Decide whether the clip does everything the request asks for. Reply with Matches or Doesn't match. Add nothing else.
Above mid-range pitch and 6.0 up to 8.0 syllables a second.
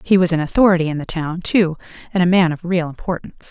Doesn't match